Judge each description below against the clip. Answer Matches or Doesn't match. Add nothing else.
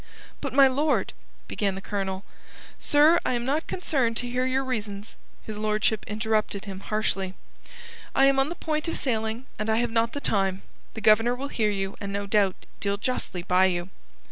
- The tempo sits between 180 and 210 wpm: Matches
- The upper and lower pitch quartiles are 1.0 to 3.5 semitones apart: Doesn't match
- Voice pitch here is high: Matches